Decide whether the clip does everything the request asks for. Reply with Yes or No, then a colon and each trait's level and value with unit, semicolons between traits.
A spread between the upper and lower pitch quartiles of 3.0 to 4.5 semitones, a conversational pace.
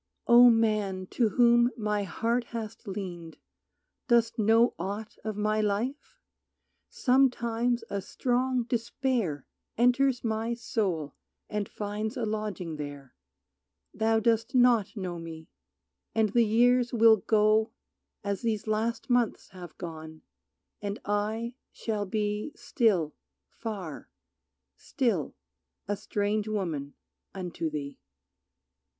No: average, 3.4 semitones; slow, 110 wpm